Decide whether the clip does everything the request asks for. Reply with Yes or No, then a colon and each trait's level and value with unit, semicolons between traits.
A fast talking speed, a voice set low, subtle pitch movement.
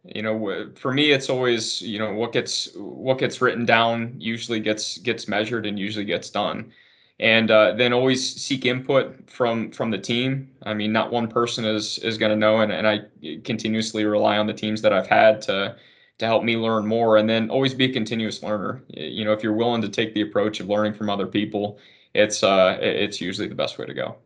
Yes: fast, 220 wpm; low, 110 Hz; narrow, 1.7 semitones